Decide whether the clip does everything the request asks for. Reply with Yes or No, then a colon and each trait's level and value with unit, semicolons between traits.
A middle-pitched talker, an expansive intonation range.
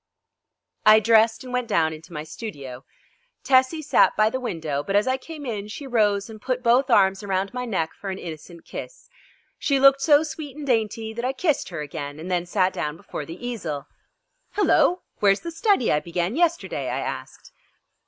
No: high, 220 Hz; wide, 7.0 semitones